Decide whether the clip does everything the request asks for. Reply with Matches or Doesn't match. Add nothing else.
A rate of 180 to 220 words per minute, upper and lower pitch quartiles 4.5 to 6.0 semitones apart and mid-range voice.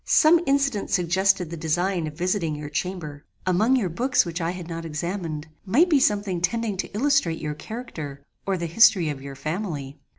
Matches